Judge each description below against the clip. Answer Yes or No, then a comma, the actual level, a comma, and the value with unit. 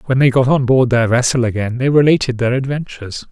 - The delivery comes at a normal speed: No, fast, 215 wpm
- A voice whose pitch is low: Yes, low, 125 Hz